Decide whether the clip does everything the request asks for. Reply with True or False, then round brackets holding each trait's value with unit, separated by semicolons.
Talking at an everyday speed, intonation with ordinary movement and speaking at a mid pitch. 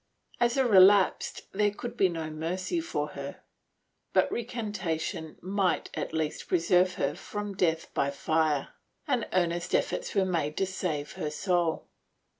True (145 wpm; 3.9 semitones; 180 Hz)